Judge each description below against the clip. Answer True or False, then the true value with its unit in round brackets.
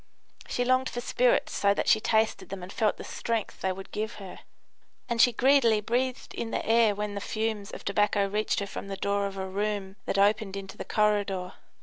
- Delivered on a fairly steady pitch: True (2.3 semitones)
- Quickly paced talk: True (215 wpm)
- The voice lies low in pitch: False (210 Hz)